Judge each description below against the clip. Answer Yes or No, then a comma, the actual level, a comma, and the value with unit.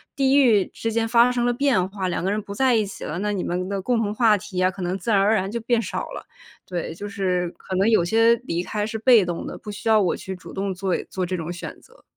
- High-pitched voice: Yes, high, 205 Hz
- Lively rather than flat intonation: No, average, 3.6 semitones